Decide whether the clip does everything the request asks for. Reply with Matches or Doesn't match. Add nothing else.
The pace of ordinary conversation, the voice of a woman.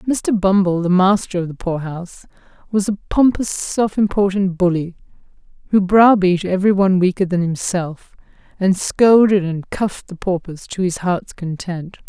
Matches